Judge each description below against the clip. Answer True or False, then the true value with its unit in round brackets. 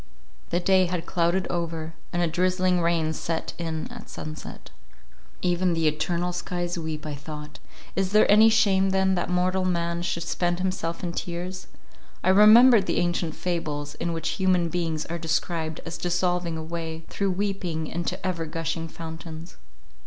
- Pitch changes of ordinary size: False (2.1 semitones)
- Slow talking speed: False (160 wpm)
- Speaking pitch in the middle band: True (175 Hz)